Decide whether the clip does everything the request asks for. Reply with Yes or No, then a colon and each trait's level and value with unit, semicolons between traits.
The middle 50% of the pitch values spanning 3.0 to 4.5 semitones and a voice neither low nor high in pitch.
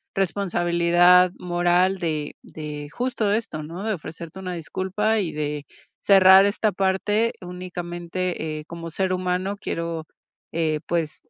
No: narrow, 2.4 semitones; medium, 180 Hz